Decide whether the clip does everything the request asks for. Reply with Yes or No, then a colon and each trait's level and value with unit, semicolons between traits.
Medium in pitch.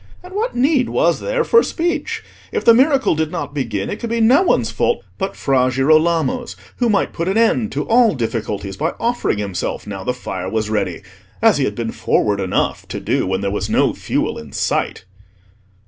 Yes: medium, 160 Hz